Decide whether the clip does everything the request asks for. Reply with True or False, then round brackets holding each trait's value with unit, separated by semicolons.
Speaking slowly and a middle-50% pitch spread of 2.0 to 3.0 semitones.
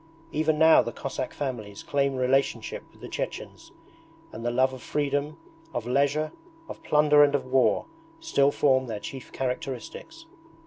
False (150 wpm; 2.5 semitones)